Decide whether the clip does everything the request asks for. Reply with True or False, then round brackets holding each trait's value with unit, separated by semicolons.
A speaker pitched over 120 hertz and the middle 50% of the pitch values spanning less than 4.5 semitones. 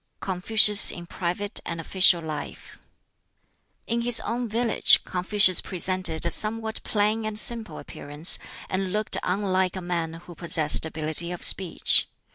True (185 Hz; 3.8 semitones)